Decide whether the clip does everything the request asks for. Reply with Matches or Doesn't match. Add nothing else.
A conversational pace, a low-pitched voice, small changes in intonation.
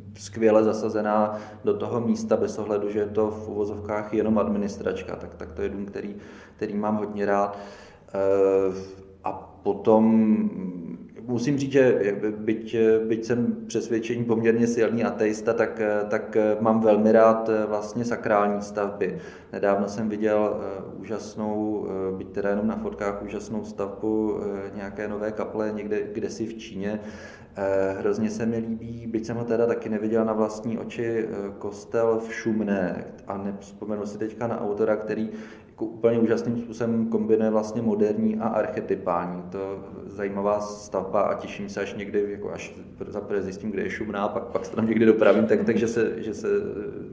Matches